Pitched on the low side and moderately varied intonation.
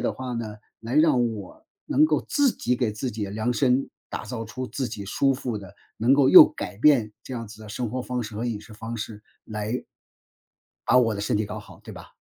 Yes: low, 115 Hz; average, 3.1 semitones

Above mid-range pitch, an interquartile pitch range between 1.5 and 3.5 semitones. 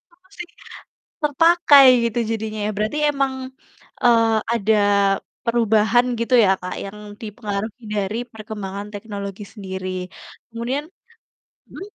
Yes: high, 220 Hz; average, 3.2 semitones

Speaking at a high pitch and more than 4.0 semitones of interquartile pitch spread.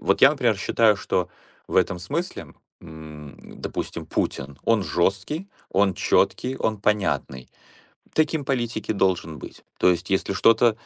No: low, 100 Hz; average, 5.3 semitones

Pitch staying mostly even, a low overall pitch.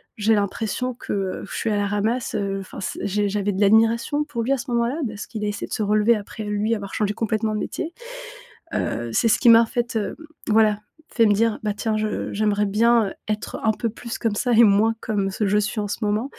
No: narrow, 2.0 semitones; high, 215 Hz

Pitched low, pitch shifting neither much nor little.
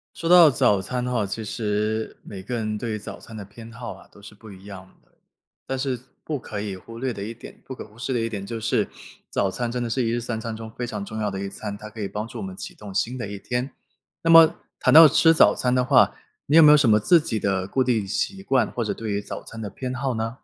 Yes: low, 115 Hz; average, 3.6 semitones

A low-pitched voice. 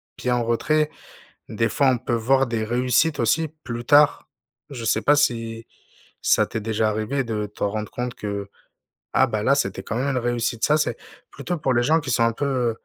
Yes: low, 120 Hz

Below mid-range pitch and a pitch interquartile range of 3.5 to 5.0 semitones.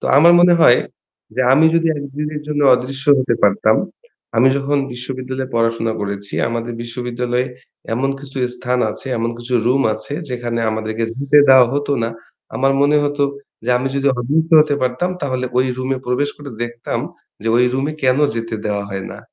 No: low, 130 Hz; average, 3.0 semitones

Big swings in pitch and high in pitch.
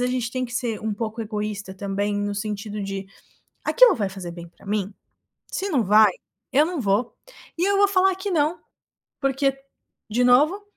Yes: wide, 5.8 semitones; high, 225 Hz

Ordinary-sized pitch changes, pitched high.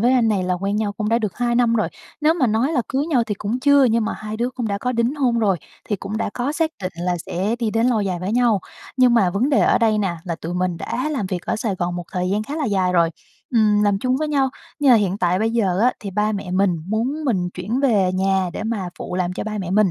Yes: average, 4.4 semitones; high, 215 Hz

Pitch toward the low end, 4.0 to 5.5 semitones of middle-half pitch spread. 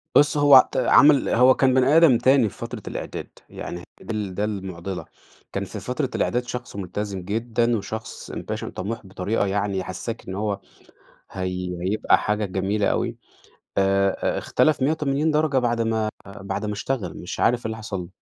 Yes: low, 105 Hz; average, 4.3 semitones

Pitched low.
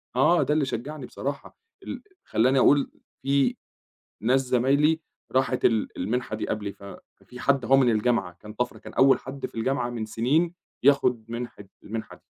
Yes: low, 125 Hz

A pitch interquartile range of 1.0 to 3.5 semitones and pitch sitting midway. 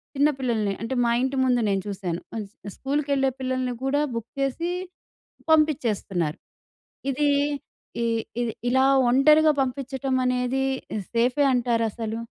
No: average, 2.9 semitones; very high, 255 Hz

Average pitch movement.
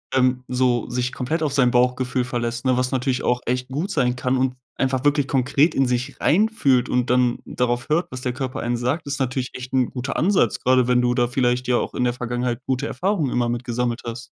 No: narrow, 1.4 semitones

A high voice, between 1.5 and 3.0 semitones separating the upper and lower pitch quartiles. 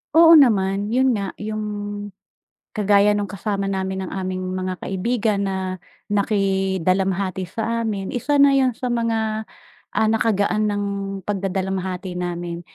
Yes: high, 200 Hz; average, 2.7 semitones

